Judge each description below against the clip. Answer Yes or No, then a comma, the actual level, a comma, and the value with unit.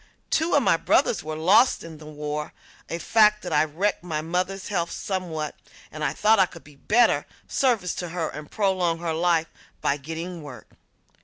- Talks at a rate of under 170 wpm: No, average, 185 wpm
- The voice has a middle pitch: Yes, medium, 170 Hz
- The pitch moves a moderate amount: Yes, average, 3.7 semitones